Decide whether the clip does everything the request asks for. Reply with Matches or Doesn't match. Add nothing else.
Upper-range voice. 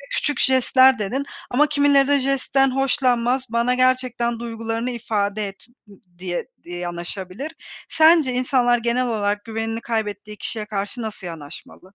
Matches